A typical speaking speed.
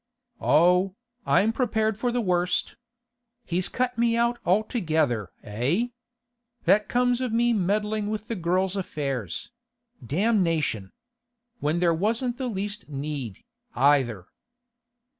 No: slow, 110 wpm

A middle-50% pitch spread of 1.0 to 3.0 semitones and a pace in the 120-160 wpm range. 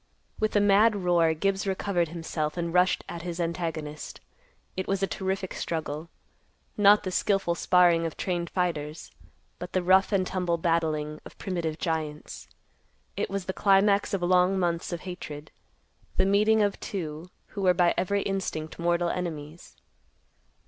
Yes: average, 2.7 semitones; average, 155 wpm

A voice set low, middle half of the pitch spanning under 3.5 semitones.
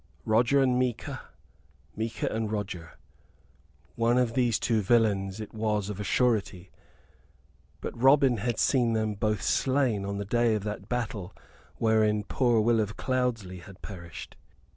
Yes: low, 110 Hz; average, 2.9 semitones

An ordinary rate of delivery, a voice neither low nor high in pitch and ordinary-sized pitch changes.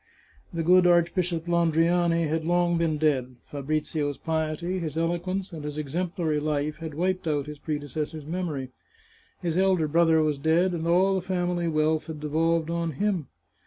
No: average, 160 wpm; medium, 165 Hz; narrow, 2.2 semitones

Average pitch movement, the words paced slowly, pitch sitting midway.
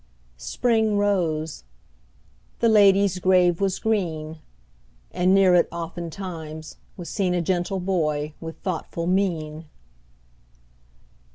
Yes: average, 3.2 semitones; slow, 100 wpm; medium, 180 Hz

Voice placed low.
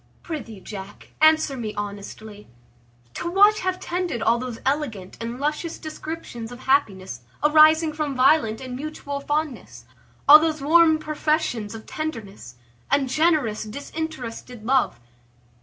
No: very high, 280 Hz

